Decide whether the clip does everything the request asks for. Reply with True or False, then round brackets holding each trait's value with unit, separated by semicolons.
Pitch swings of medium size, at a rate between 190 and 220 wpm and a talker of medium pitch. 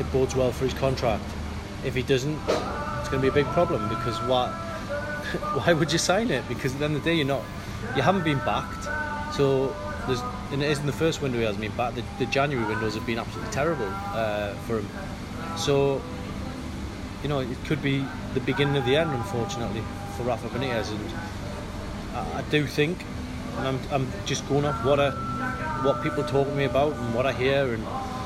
False (4.7 semitones; 200 wpm; 125 Hz)